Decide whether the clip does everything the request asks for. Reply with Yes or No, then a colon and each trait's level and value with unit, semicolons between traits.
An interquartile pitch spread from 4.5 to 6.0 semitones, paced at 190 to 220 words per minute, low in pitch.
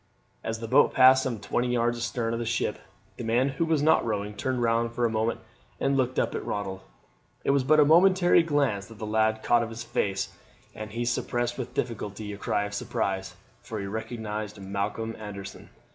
No: average, 3.4 semitones; fast, 205 wpm; low, 115 Hz